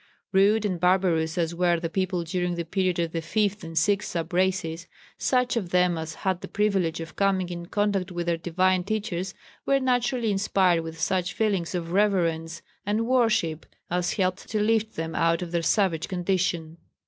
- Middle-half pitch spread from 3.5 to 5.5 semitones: No, average, 3.1 semitones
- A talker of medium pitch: Yes, medium, 180 Hz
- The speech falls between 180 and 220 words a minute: Yes, average, 185 wpm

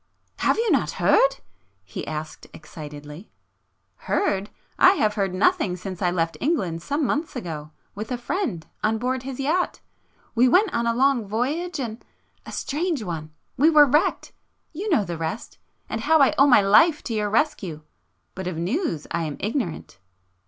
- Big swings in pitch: Yes, wide, 8.8 semitones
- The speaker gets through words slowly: No, average, 165 wpm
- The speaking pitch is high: Yes, high, 225 Hz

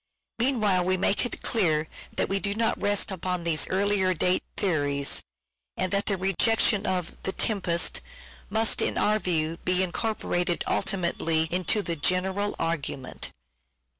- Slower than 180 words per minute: Yes, average, 150 wpm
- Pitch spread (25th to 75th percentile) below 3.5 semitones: Yes, average, 3.1 semitones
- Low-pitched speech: No, medium, 185 Hz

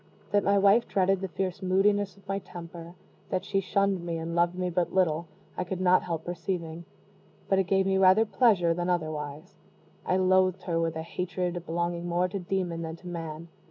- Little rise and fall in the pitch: Yes, narrow, 2.2 semitones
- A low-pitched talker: No, medium, 180 Hz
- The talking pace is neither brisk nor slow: Yes, average, 195 wpm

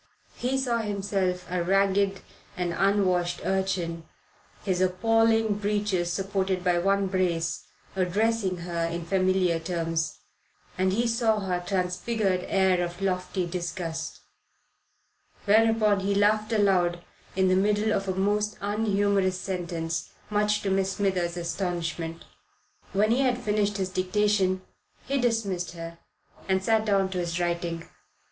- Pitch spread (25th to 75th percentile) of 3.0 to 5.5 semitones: No, narrow, 2.6 semitones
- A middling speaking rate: No, slow, 130 wpm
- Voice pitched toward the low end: No, high, 190 Hz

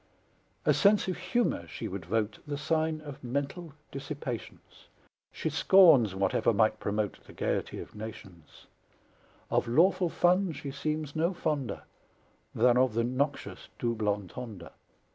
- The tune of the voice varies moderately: No, wide, 6.5 semitones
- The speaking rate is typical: No, slow, 130 wpm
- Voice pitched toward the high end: No, low, 135 Hz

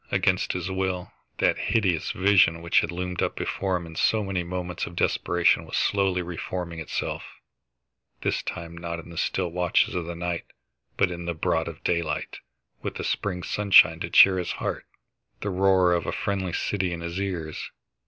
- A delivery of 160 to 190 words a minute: Yes, average, 180 wpm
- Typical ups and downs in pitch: No, narrow, 1.8 semitones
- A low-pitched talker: Yes, very low, 90 Hz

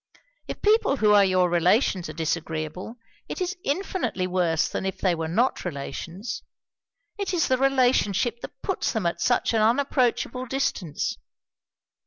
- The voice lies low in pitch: No, high, 210 Hz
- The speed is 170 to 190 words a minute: No, average, 150 wpm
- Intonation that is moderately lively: No, wide, 6.9 semitones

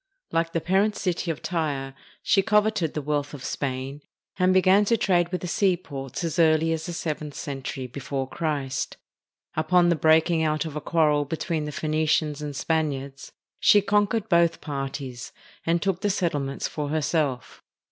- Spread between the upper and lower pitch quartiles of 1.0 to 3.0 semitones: No, average, 3.4 semitones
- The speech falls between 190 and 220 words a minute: No, average, 165 wpm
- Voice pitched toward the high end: No, medium, 160 Hz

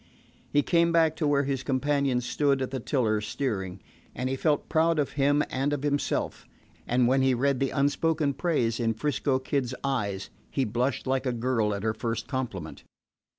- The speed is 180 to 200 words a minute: Yes, average, 185 wpm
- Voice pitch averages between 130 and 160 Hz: Yes, low, 135 Hz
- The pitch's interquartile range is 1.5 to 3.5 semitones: Yes, average, 3.1 semitones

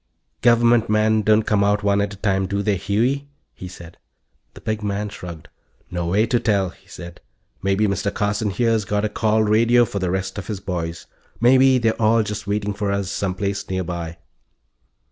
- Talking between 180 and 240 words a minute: Yes, average, 190 wpm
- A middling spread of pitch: No, narrow, 2.2 semitones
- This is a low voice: Yes, low, 105 Hz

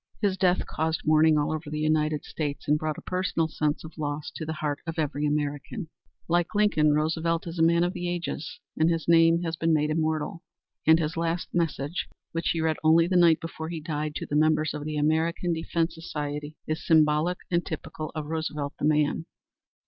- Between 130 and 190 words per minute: No, fast, 205 wpm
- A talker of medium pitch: Yes, medium, 160 Hz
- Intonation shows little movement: Yes, narrow, 1.7 semitones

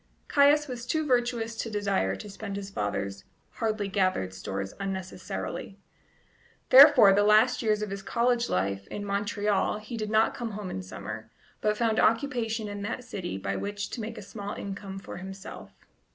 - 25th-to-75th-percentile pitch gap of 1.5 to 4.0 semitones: Yes, average, 3.0 semitones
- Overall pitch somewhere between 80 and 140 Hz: No, high, 205 Hz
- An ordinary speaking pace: Yes, average, 170 wpm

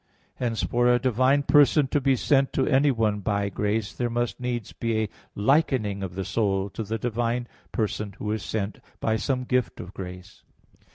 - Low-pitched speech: Yes, low, 115 Hz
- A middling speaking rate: Yes, average, 180 wpm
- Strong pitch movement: No, average, 3.7 semitones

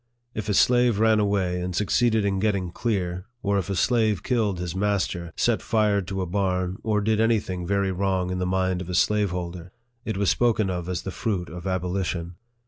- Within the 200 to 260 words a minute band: Yes, fast, 205 wpm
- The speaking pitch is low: Yes, very low, 95 Hz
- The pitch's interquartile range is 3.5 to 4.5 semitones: No, average, 2.7 semitones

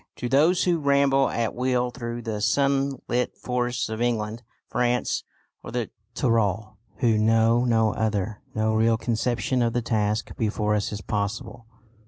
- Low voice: Yes, low, 115 Hz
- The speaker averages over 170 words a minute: No, average, 150 wpm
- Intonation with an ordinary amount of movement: No, narrow, 2.2 semitones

